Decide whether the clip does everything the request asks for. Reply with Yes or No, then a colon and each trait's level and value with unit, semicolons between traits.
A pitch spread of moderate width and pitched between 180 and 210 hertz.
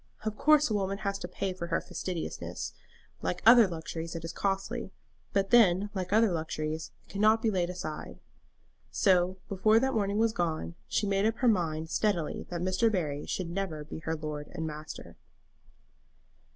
Yes: average, 4.2 semitones; medium, 185 Hz